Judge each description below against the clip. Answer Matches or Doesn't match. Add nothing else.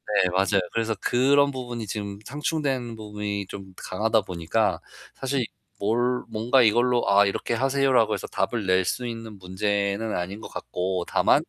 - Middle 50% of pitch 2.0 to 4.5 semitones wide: Matches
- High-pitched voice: Doesn't match